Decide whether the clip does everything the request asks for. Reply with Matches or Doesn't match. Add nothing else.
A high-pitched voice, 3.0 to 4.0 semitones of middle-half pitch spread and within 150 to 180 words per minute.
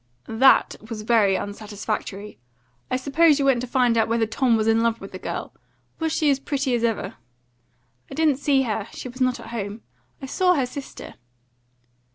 Doesn't match